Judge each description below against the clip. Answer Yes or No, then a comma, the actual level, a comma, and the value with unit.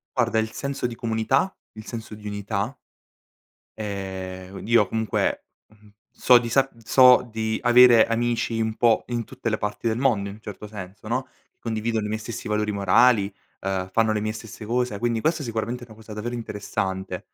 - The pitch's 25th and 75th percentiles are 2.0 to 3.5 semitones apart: Yes, narrow, 2.4 semitones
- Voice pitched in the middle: No, low, 110 Hz